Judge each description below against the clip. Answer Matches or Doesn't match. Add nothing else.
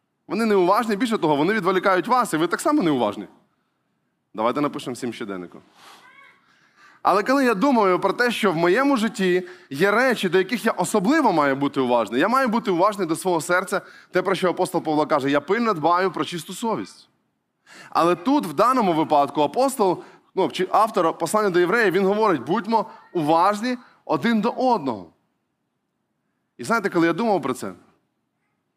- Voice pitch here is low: Doesn't match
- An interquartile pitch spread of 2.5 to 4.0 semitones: Doesn't match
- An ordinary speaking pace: Doesn't match